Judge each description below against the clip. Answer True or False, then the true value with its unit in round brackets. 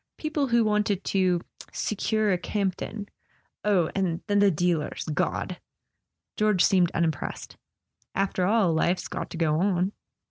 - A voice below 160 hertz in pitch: False (190 Hz)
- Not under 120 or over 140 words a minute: True (135 wpm)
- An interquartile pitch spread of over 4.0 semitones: False (3.2 semitones)